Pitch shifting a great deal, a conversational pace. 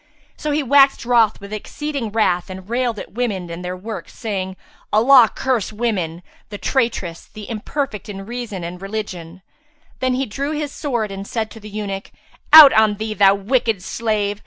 No: average, 4.1 semitones; average, 175 wpm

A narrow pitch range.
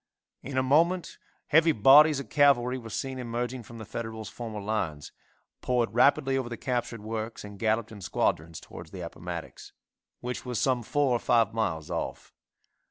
No: average, 3.3 semitones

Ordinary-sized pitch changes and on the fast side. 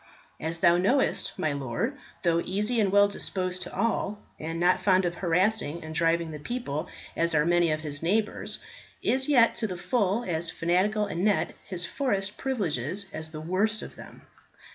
No: average, 4.1 semitones; average, 175 wpm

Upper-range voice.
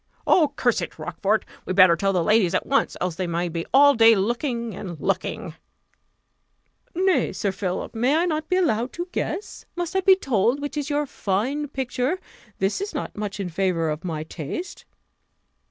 Yes: high, 230 Hz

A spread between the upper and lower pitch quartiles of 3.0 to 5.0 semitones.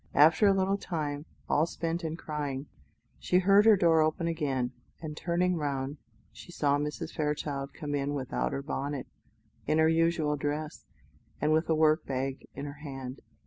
No: narrow, 2.6 semitones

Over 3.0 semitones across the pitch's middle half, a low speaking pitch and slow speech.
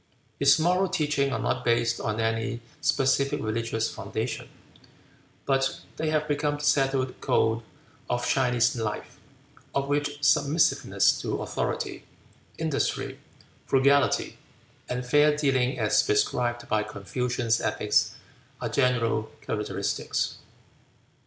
Yes: average, 3.7 semitones; low, 130 Hz; slow, 110 wpm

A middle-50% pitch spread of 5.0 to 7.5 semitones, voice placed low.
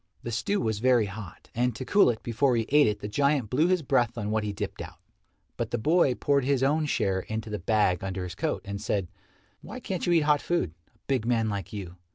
Yes: wide, 5.5 semitones; low, 115 Hz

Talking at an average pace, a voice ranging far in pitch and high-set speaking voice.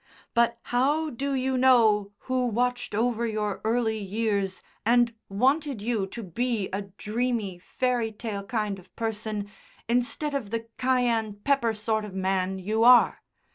No: average, 145 wpm; average, 3.1 semitones; high, 225 Hz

